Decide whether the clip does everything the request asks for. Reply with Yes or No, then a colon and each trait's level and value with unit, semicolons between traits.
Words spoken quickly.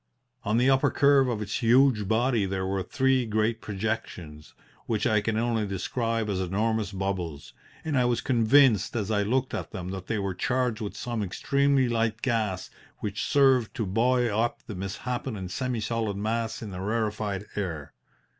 No: average, 175 wpm